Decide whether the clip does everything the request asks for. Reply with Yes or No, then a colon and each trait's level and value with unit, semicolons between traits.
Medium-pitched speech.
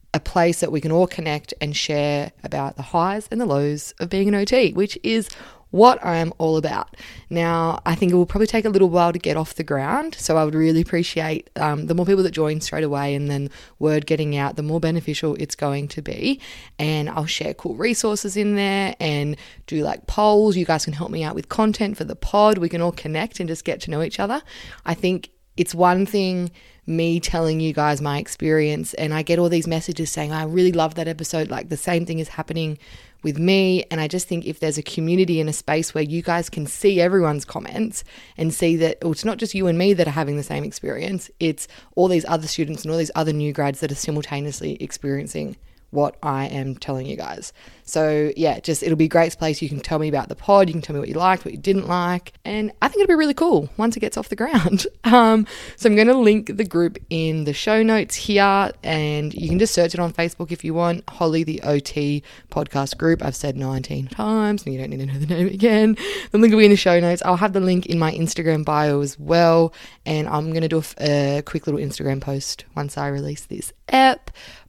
Yes: medium, 165 Hz